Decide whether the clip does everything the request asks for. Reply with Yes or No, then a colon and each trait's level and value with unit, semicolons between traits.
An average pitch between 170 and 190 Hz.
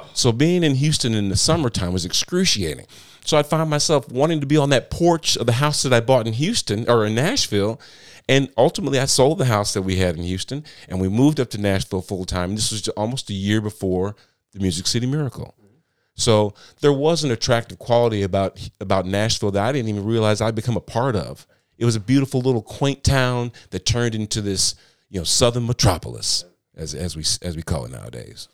No: low, 115 Hz